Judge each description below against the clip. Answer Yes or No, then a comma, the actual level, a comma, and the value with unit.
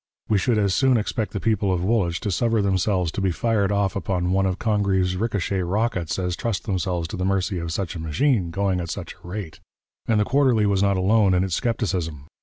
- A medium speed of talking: No, fast, 220 wpm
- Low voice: Yes, very low, 95 Hz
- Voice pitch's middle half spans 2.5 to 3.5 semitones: Yes, average, 2.9 semitones